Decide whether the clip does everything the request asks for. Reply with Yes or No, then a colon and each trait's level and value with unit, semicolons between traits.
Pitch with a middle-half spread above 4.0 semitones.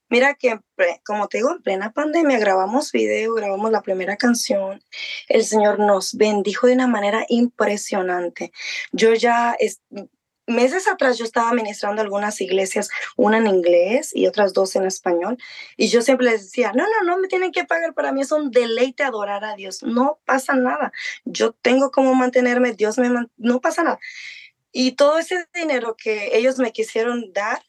Yes: average, 4.6 semitones